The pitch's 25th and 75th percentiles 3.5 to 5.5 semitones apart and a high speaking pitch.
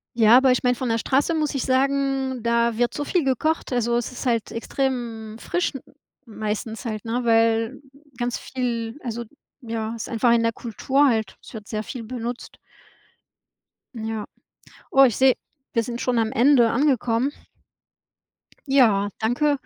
No: narrow, 2.6 semitones; high, 240 Hz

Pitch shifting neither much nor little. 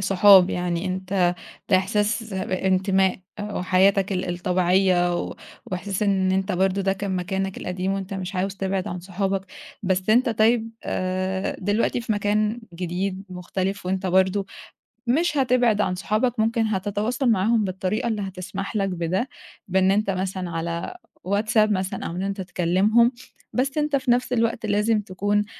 No: narrow, 2.3 semitones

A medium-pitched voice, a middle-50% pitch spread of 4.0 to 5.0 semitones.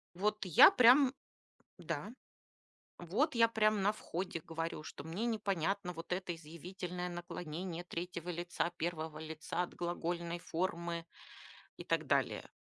No: medium, 175 Hz; average, 2.8 semitones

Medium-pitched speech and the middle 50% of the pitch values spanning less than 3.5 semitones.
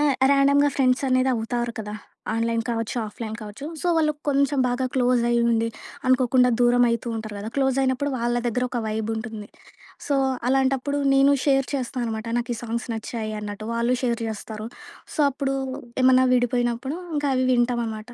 No: high, 245 Hz; average, 2.7 semitones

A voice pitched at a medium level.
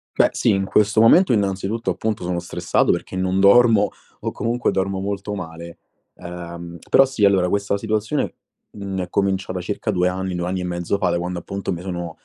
No: very low, 95 Hz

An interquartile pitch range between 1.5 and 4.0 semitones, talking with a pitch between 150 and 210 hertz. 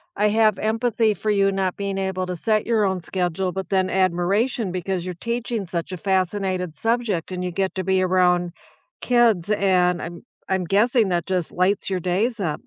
Yes: narrow, 2.6 semitones; high, 190 Hz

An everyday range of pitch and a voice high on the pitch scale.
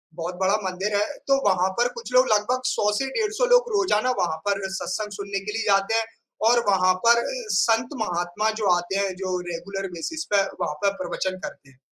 Yes: average, 3.9 semitones; high, 200 Hz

